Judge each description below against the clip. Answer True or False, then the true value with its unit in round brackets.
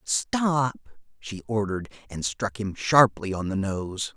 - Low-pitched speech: True (105 Hz)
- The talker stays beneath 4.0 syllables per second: True (3.6 syllables/s)